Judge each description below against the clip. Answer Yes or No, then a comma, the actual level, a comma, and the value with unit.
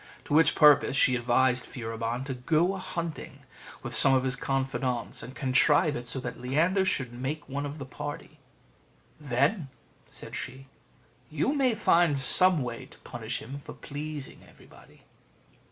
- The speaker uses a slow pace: No, average, 155 wpm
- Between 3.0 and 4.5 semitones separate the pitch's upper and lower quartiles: Yes, average, 3.5 semitones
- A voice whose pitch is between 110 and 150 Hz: Yes, low, 135 Hz